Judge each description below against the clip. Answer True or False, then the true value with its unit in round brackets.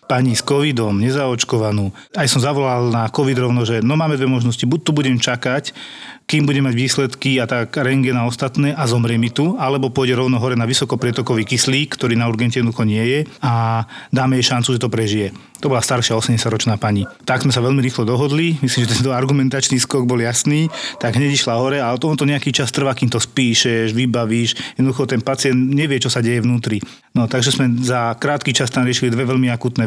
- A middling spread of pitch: False (2.3 semitones)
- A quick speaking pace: True (205 wpm)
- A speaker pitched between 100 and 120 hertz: False (130 Hz)